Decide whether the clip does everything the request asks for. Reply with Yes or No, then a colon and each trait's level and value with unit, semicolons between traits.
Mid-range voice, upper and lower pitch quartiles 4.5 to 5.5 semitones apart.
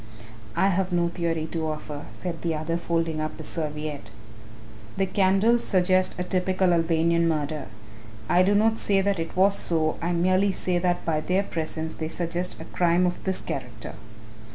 No: medium, 170 Hz; average, 2.7 semitones